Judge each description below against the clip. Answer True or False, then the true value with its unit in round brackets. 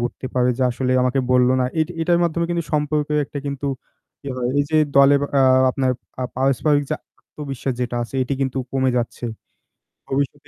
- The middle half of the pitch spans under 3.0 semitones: True (2.6 semitones)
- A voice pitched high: False (135 Hz)